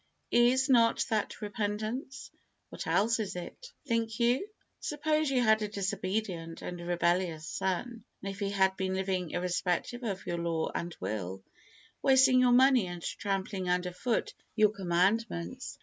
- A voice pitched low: No, high, 200 Hz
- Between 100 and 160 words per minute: Yes, average, 145 wpm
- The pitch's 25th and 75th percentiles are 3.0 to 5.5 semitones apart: Yes, average, 5.0 semitones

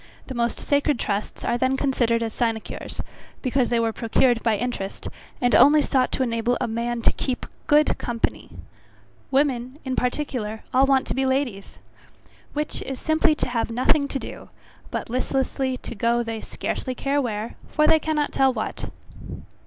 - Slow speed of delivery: No, average, 170 wpm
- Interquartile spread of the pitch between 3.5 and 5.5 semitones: No, average, 2.8 semitones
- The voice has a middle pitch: No, very high, 250 Hz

